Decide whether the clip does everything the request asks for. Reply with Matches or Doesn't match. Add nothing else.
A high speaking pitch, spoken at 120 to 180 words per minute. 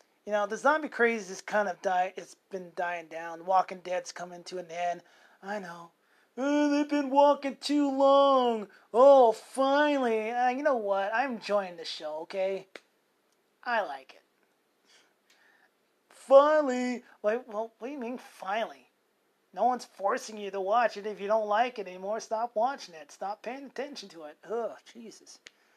Matches